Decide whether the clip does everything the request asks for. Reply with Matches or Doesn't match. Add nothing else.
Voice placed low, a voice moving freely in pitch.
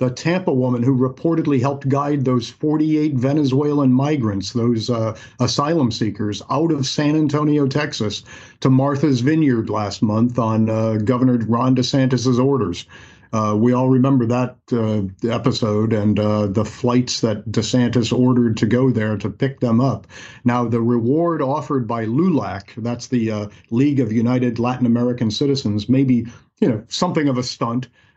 Doesn't match